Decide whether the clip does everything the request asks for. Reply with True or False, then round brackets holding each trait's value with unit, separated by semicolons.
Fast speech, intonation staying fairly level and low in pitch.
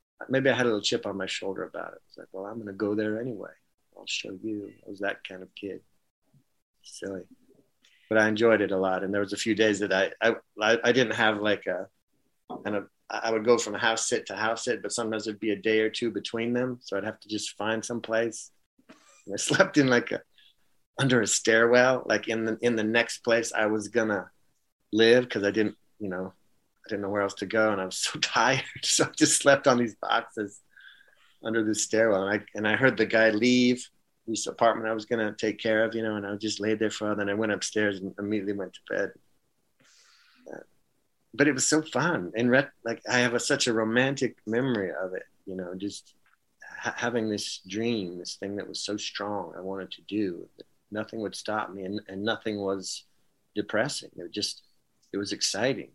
True (225 wpm; 2.2 semitones; 110 Hz)